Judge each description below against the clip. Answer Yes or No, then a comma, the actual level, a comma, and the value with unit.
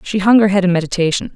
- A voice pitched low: No, high, 190 Hz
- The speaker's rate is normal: No, fast, 265 wpm